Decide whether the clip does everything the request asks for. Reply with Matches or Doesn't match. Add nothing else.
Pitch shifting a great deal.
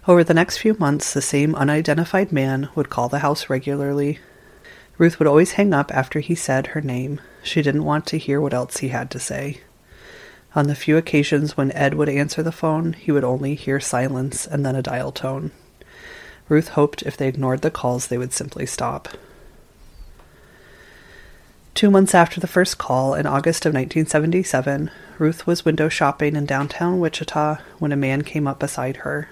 Doesn't match